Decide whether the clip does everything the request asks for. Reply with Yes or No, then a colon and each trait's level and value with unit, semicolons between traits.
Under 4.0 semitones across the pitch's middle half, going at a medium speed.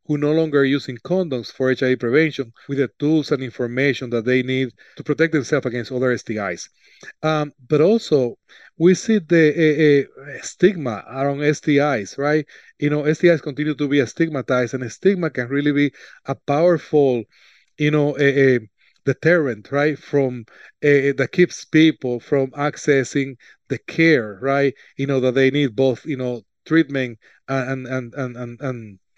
Yes: average, 2.8 semitones; average, 160 wpm